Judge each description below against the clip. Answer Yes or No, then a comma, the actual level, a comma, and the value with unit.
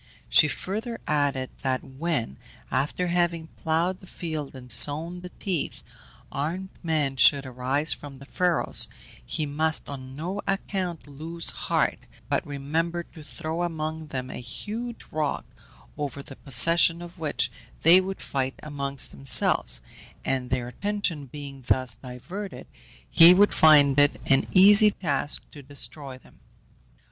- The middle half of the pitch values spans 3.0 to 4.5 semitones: Yes, average, 4.2 semitones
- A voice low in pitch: No, medium, 150 Hz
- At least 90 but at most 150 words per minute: Yes, average, 140 wpm